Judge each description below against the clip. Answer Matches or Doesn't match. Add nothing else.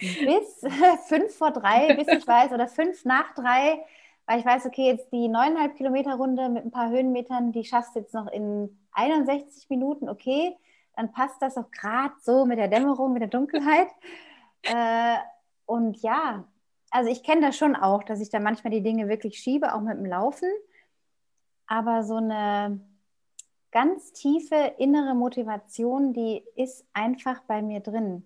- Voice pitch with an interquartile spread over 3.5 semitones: Matches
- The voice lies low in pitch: Doesn't match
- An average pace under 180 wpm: Matches